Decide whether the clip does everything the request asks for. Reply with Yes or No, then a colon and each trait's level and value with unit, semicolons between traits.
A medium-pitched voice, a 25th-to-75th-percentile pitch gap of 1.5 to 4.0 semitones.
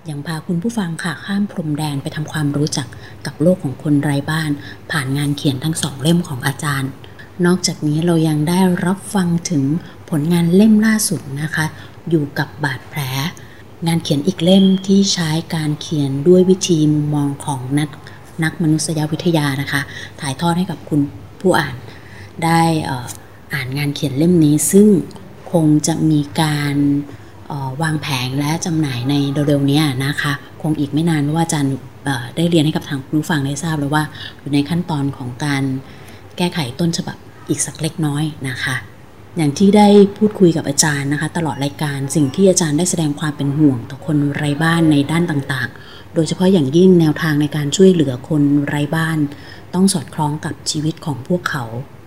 Yes: medium, 150 Hz; average, 3.0 semitones